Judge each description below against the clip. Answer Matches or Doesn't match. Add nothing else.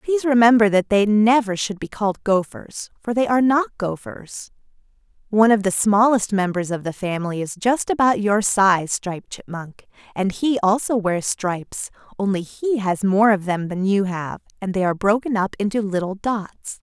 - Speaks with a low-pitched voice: Doesn't match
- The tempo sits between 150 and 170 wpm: Doesn't match